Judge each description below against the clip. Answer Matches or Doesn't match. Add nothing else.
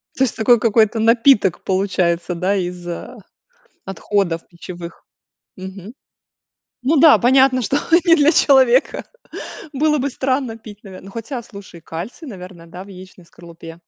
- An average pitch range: Doesn't match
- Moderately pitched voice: Doesn't match